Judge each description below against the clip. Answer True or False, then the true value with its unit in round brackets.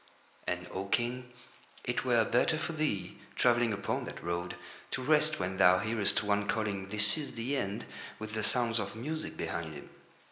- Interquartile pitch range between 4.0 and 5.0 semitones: True (4.3 semitones)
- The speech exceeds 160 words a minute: True (175 wpm)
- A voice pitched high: False (110 Hz)